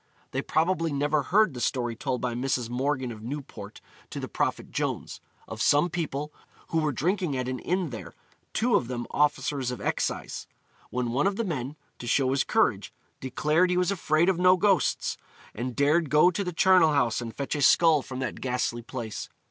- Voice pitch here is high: No, medium, 145 Hz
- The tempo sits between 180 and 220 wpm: Yes, average, 195 wpm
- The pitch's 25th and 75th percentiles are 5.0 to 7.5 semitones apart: Yes, average, 5.3 semitones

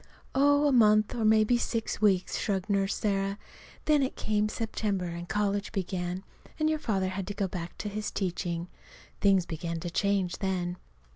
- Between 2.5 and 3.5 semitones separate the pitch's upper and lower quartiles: Yes, average, 2.8 semitones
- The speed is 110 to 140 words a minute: No, average, 170 wpm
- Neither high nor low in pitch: No, high, 200 Hz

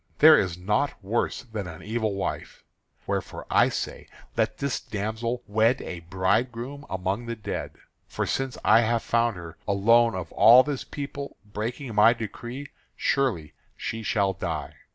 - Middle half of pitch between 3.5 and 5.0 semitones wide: Yes, average, 3.8 semitones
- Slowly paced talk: No, average, 155 wpm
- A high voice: No, low, 115 Hz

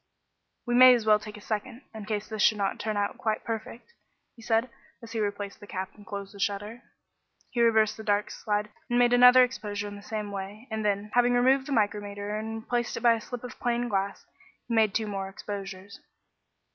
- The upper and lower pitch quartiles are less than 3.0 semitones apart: Yes, narrow, 2.6 semitones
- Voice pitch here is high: Yes, high, 215 Hz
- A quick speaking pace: Yes, fast, 215 wpm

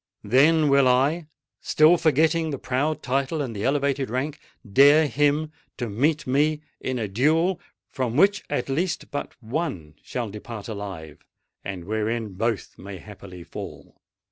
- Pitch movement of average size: No, wide, 5.8 semitones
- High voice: No, low, 135 Hz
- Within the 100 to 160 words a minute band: Yes, average, 140 wpm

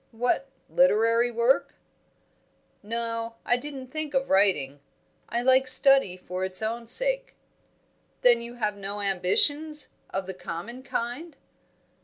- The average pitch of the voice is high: Yes, high, 235 Hz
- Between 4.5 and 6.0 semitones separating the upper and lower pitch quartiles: Yes, average, 4.9 semitones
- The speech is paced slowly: Yes, slow, 125 wpm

